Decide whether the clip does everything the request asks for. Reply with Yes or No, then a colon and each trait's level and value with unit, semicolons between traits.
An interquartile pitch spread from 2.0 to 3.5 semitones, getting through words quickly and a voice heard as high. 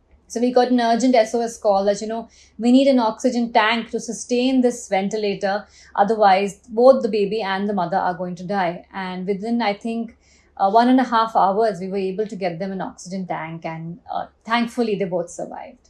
Yes: average, 3.2 semitones; fast, 210 wpm; high, 215 Hz